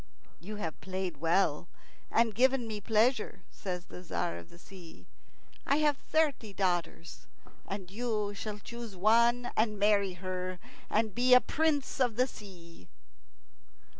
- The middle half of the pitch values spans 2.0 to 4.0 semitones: No, average, 4.5 semitones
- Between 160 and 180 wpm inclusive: No, average, 140 wpm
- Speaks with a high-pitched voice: Yes, high, 205 Hz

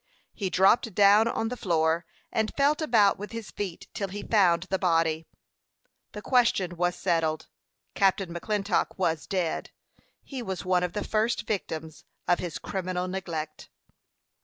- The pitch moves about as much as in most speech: Yes, average, 3.5 semitones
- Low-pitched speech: No, high, 190 Hz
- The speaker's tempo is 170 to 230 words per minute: No, average, 150 wpm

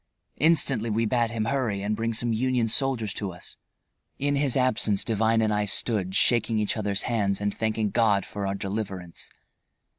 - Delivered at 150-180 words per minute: Yes, average, 175 wpm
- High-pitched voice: No, low, 110 Hz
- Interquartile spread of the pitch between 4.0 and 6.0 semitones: No, narrow, 2.6 semitones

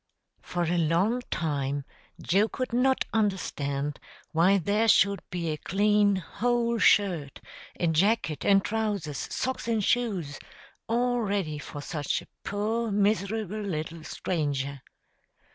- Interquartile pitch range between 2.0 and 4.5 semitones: No, wide, 5.5 semitones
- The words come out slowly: Yes, slow, 125 wpm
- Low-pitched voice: No, high, 195 Hz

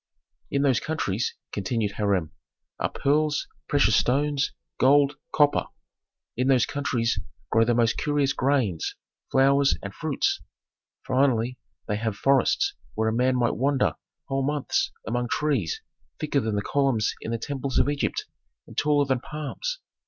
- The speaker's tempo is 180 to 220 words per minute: No, average, 145 wpm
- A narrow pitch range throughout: No, average, 4.0 semitones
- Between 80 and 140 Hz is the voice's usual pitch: Yes, low, 135 Hz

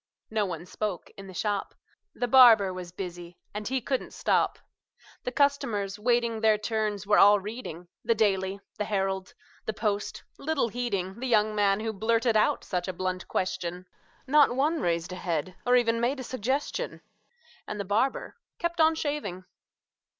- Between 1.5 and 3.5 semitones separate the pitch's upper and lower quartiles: No, average, 4.3 semitones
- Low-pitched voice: No, high, 210 Hz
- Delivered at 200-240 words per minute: No, average, 165 wpm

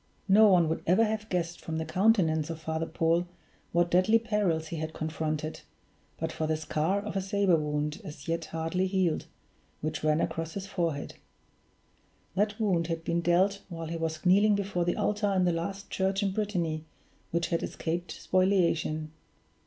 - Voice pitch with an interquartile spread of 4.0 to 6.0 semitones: No, average, 3.4 semitones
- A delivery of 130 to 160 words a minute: No, average, 175 wpm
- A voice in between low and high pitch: Yes, medium, 170 Hz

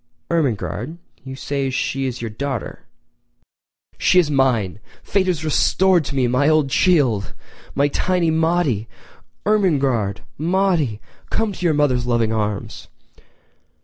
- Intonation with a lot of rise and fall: Yes, wide, 5.8 semitones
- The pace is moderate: No, slow, 115 wpm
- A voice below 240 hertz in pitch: Yes, medium, 140 Hz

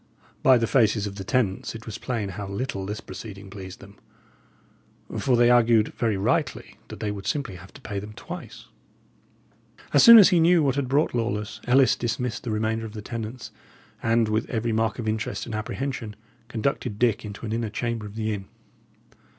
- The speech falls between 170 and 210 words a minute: Yes, average, 190 wpm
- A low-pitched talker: Yes, low, 110 Hz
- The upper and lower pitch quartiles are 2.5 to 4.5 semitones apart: Yes, average, 2.8 semitones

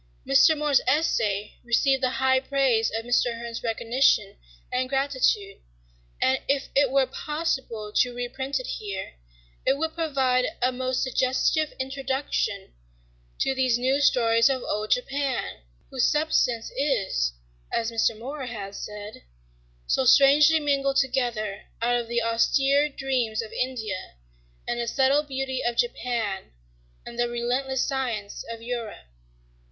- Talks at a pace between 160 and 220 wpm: No, slow, 135 wpm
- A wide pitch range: No, average, 3.0 semitones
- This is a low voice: No, very high, 255 Hz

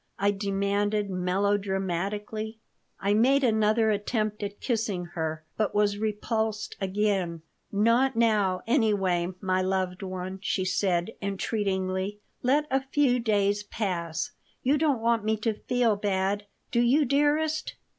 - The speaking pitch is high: Yes, high, 205 Hz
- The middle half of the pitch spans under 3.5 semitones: Yes, average, 2.9 semitones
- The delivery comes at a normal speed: No, slow, 125 wpm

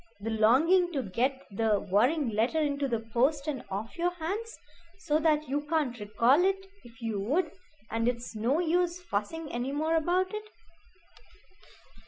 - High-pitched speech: Yes, very high, 280 Hz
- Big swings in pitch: Yes, wide, 6.4 semitones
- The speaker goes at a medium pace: Yes, average, 160 wpm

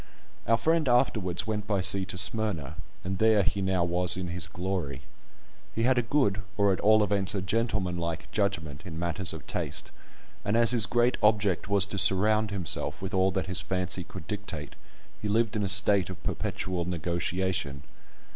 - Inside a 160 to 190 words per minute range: Yes, average, 185 wpm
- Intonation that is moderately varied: Yes, average, 3.0 semitones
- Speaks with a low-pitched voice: Yes, very low, 95 Hz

